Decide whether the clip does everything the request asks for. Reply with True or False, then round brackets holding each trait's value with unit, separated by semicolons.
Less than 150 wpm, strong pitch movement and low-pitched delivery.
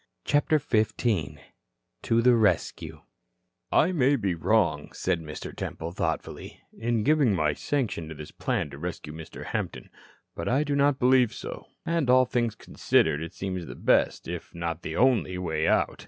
False (165 wpm; 7.8 semitones; 105 Hz)